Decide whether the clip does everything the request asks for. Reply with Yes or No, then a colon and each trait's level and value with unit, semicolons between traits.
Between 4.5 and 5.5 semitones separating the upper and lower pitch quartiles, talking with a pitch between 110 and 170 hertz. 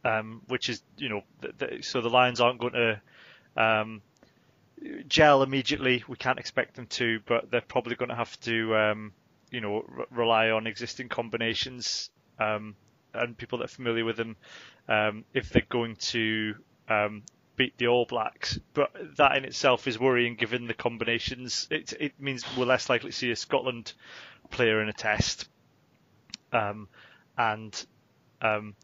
No: narrow, 2.4 semitones; low, 115 Hz